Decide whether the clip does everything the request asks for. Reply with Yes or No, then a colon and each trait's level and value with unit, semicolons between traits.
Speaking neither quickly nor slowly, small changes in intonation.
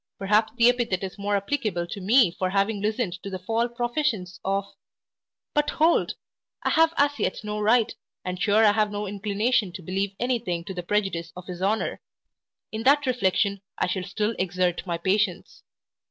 No: average, 185 wpm; average, 3.3 semitones